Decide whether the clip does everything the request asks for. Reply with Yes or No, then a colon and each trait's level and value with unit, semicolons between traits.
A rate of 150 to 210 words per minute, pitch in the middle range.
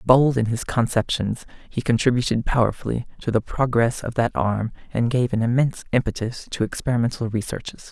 No: average, 160 wpm; low, 120 Hz